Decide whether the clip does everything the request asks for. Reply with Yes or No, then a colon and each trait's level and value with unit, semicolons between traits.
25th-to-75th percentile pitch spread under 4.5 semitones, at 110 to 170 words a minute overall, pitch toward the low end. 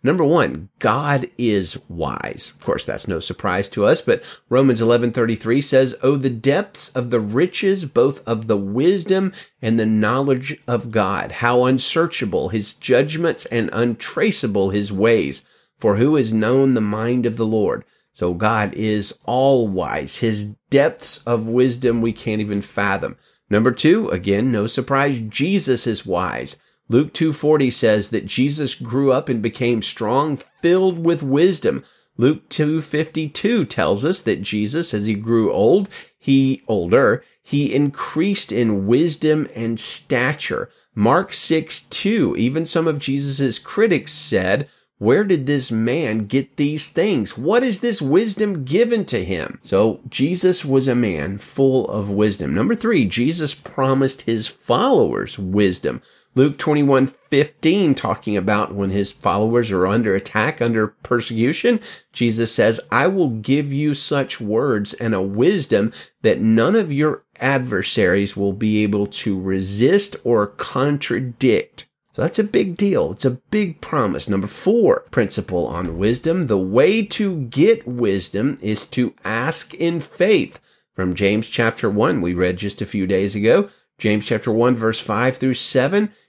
No: wide, 5.6 semitones; average, 150 wpm; low, 125 Hz